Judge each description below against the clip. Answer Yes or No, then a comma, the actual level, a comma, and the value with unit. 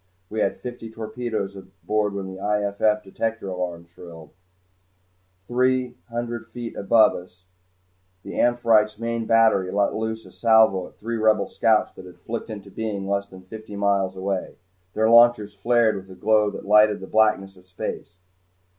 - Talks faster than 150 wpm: Yes, average, 160 wpm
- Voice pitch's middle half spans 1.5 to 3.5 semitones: Yes, average, 2.7 semitones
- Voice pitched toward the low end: Yes, low, 105 Hz